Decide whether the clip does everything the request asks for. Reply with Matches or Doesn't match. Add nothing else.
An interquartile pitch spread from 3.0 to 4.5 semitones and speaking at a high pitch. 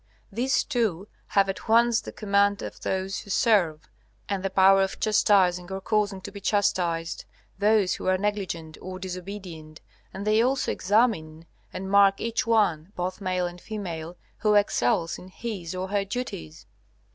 Doesn't match